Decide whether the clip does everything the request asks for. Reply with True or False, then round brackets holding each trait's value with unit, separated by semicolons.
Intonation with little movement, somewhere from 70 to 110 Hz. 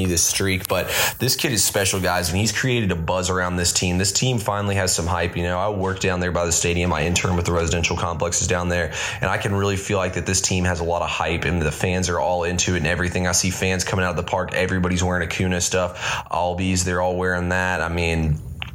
True (1.2 semitones; 90 Hz)